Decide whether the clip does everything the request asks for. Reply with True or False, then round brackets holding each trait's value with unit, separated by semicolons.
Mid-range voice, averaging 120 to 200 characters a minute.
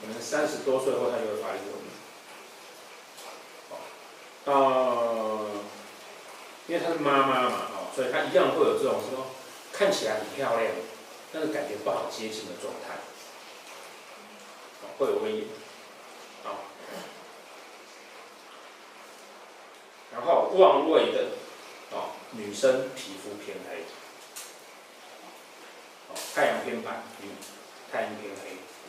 True (150 Hz; 145 characters per minute)